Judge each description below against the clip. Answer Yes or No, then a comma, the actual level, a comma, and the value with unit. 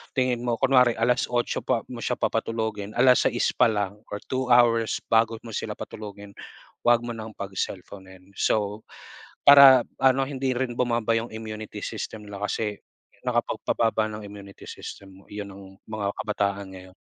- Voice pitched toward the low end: Yes, low, 110 Hz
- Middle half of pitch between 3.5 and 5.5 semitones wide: No, average, 2.8 semitones